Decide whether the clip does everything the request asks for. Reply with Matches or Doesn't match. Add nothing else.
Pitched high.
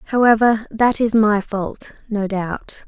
Matches